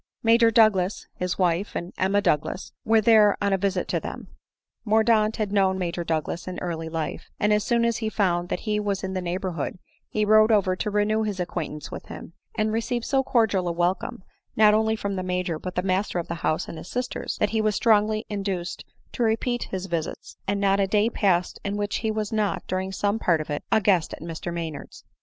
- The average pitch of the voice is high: Yes, high, 200 Hz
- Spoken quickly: Yes, fast, 225 wpm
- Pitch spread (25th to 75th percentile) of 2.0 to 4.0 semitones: Yes, average, 3.3 semitones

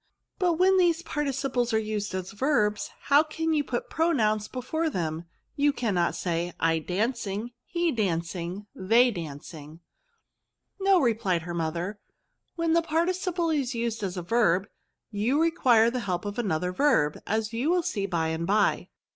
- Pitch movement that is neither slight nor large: No, wide, 8.8 semitones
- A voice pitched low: No, high, 225 Hz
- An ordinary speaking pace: Yes, average, 170 wpm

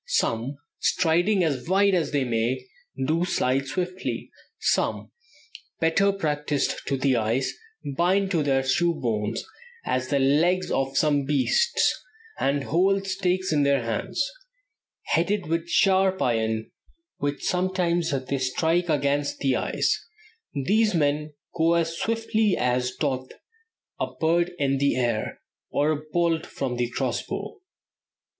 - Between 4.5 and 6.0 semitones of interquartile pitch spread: Yes, average, 5.1 semitones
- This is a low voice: No, medium, 150 Hz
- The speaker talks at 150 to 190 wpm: No, slow, 135 wpm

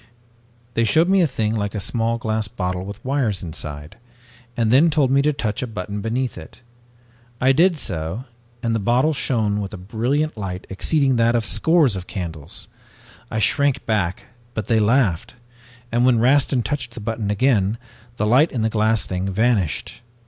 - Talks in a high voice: No, low, 115 Hz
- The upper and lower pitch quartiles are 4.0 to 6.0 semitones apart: Yes, average, 4.3 semitones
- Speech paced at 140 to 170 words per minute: No, average, 180 wpm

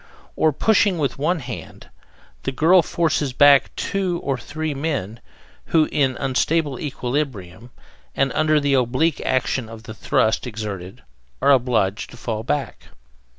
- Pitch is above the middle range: No, low, 135 Hz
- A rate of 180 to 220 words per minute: No, average, 140 wpm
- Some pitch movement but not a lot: Yes, average, 4.5 semitones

